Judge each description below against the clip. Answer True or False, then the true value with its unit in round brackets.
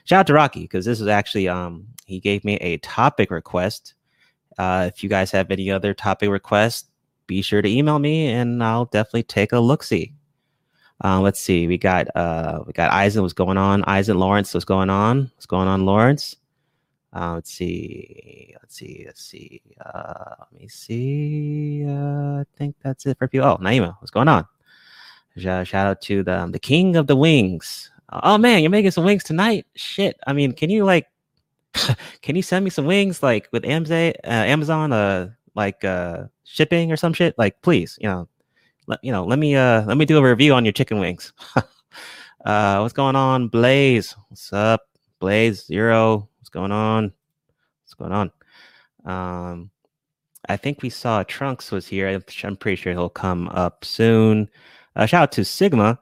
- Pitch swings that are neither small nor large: False (6.8 semitones)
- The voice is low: True (110 Hz)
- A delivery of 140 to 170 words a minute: False (185 wpm)